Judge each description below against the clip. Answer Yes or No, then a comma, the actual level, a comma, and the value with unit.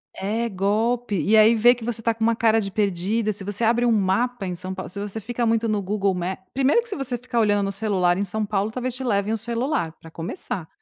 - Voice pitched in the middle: No, high, 215 Hz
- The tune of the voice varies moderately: Yes, average, 3.1 semitones